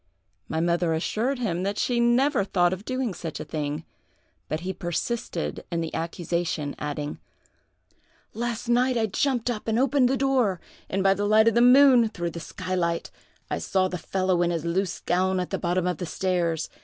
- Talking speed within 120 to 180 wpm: No, average, 190 wpm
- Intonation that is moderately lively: No, wide, 5.8 semitones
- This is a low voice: No, medium, 185 Hz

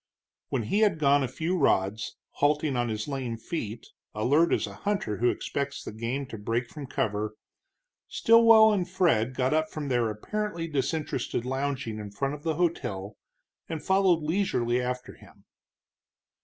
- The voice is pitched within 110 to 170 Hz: Yes, low, 135 Hz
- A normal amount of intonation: No, wide, 6.0 semitones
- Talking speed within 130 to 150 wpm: No, average, 160 wpm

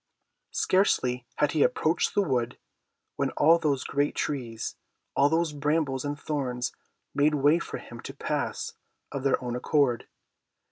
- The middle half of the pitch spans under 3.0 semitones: No, average, 3.3 semitones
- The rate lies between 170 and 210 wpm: No, average, 145 wpm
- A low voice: No, medium, 145 Hz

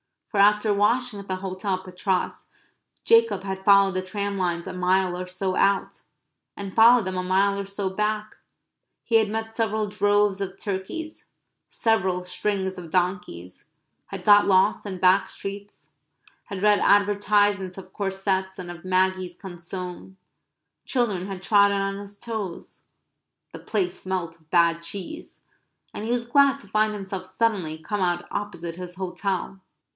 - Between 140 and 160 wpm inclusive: Yes, average, 155 wpm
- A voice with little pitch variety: Yes, narrow, 2.0 semitones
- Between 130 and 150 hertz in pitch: No, high, 195 Hz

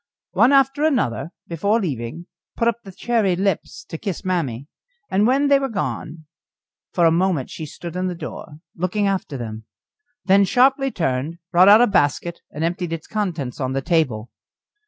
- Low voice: No, medium, 180 Hz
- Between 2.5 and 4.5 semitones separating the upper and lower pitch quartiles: No, average, 5.1 semitones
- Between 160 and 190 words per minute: Yes, average, 175 wpm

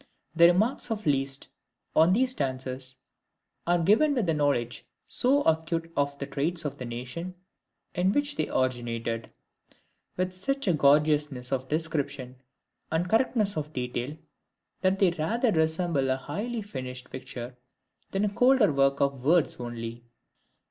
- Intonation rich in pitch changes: Yes, wide, 6.2 semitones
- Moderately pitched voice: Yes, medium, 155 Hz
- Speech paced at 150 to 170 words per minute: No, average, 140 wpm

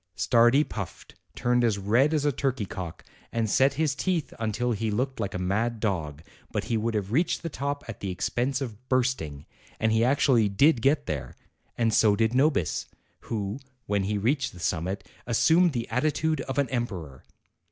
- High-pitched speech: No, low, 115 Hz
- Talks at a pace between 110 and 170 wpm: No, average, 185 wpm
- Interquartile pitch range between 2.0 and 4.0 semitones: No, average, 5.0 semitones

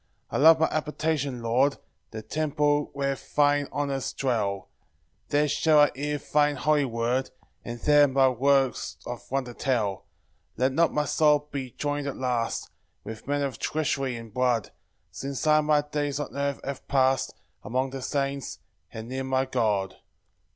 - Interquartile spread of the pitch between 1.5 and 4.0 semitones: Yes, narrow, 2.6 semitones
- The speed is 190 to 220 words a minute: No, average, 165 wpm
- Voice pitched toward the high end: No, low, 135 Hz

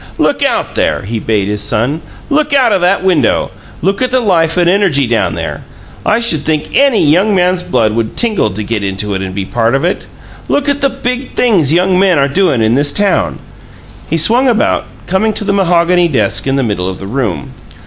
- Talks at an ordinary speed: No, fast, 215 wpm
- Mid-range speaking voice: Yes, medium, 170 Hz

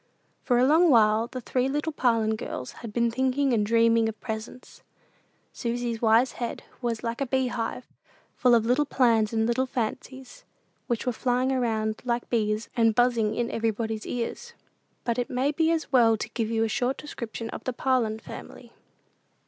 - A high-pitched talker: Yes, high, 235 Hz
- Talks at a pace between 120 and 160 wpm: No, average, 175 wpm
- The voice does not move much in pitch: Yes, narrow, 2.3 semitones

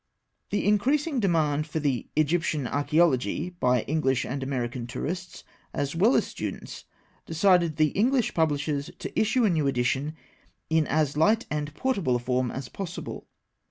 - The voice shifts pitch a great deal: No, average, 4.7 semitones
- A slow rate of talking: No, average, 150 wpm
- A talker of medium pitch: Yes, medium, 155 Hz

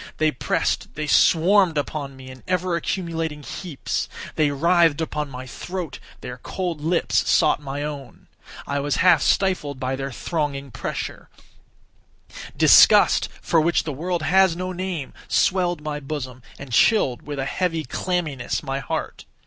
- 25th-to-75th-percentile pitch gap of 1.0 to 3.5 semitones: No, average, 4.1 semitones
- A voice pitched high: No, medium, 155 Hz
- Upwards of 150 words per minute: No, average, 145 wpm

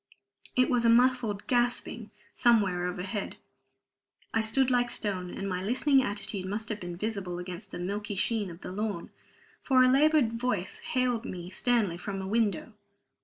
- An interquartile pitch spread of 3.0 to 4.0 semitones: No, average, 4.4 semitones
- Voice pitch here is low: No, high, 215 Hz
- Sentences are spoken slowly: No, average, 165 wpm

